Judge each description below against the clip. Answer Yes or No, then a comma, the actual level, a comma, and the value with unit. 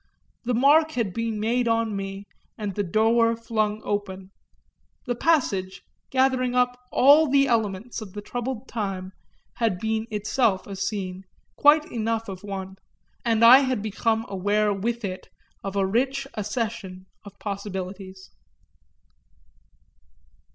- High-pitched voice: Yes, high, 215 Hz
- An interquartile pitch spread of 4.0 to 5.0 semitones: No, average, 3.5 semitones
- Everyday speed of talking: No, slow, 130 wpm